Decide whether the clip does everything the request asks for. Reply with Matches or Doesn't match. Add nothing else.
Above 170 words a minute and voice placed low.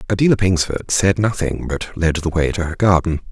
Matches